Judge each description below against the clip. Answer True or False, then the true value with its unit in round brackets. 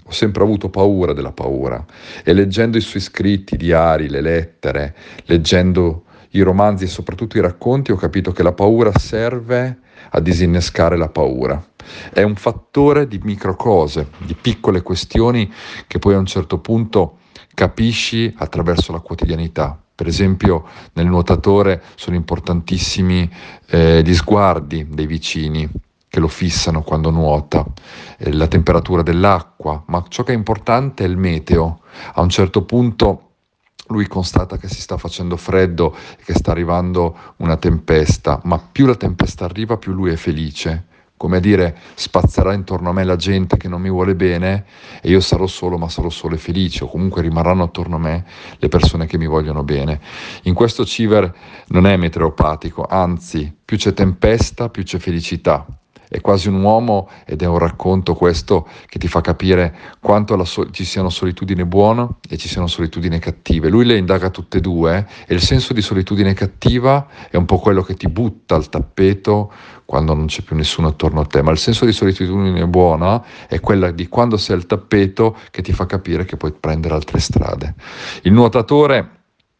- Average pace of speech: False (175 wpm)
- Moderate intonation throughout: True (3.1 semitones)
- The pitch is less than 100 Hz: True (90 Hz)